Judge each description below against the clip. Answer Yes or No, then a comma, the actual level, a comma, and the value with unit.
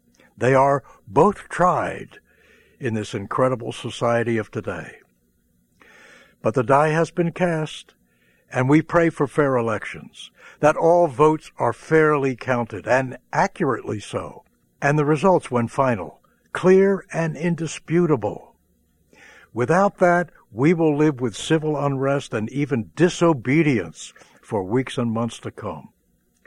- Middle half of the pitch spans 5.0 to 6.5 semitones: Yes, average, 5.3 semitones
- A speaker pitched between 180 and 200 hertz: No, medium, 140 Hz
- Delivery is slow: Yes, slow, 125 wpm